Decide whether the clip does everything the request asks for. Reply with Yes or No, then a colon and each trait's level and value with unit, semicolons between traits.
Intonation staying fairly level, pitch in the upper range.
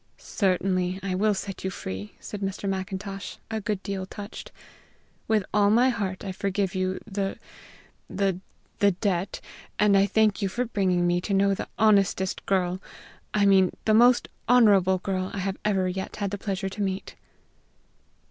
Yes: narrow, 1.6 semitones; high, 195 Hz